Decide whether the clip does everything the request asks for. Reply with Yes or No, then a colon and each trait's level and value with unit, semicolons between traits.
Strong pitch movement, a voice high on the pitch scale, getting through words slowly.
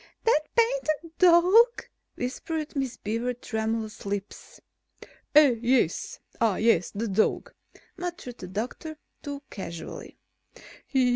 Yes: wide, 6.7 semitones; very high, 250 Hz; slow, 100 wpm